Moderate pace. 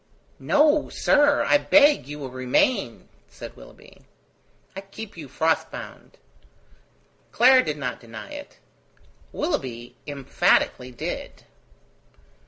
No: slow, 105 wpm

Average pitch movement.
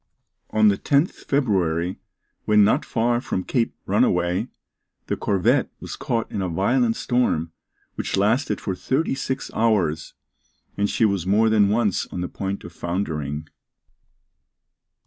Yes: average, 4.7 semitones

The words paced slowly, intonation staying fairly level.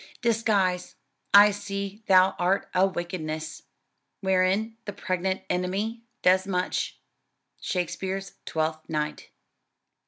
Yes: slow, 95 wpm; narrow, 1.9 semitones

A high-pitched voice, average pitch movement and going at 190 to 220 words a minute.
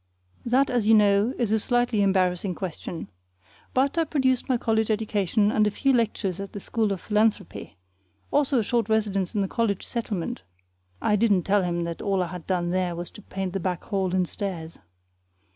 Yes: high, 205 Hz; average, 3.6 semitones; average, 195 wpm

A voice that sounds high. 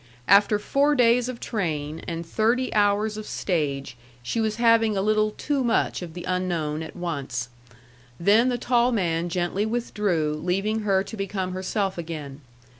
Yes: high, 195 Hz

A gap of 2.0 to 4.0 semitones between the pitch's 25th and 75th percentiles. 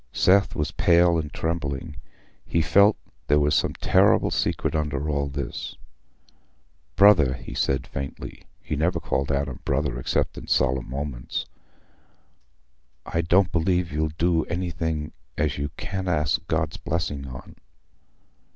Yes: average, 3.6 semitones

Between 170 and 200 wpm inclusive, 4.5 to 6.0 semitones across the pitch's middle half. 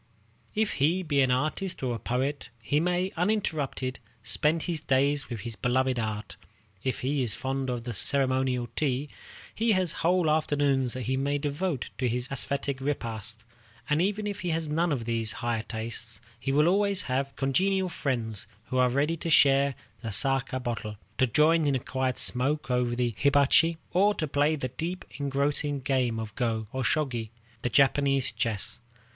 No: average, 175 wpm; average, 3.7 semitones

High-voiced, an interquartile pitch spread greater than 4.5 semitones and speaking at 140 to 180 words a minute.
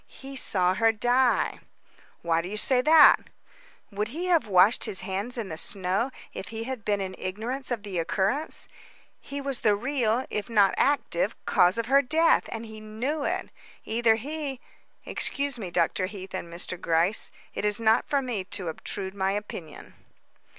Yes: high, 220 Hz; wide, 5.4 semitones; average, 175 wpm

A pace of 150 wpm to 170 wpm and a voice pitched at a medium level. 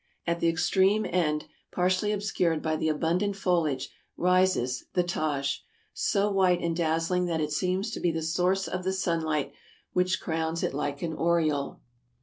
Yes: average, 160 wpm; medium, 170 Hz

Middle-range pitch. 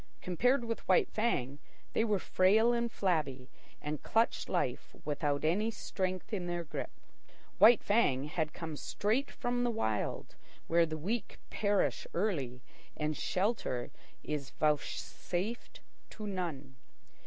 Yes: medium, 180 Hz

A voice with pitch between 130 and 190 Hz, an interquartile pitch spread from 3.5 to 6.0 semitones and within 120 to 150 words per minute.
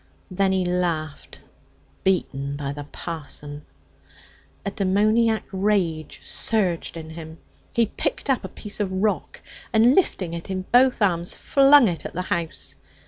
Yes: medium, 185 Hz; average, 4.6 semitones; average, 140 wpm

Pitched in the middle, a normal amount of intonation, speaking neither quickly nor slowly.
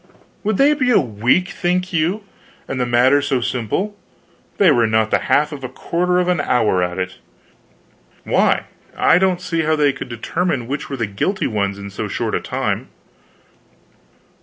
No: medium, 145 Hz; wide, 7.6 semitones; average, 180 wpm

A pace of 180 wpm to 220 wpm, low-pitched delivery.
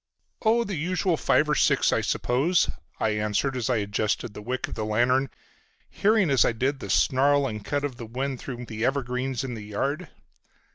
Yes: average, 195 wpm; low, 130 Hz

